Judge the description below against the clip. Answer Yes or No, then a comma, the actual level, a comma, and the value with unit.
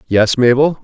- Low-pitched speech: Yes, low, 125 Hz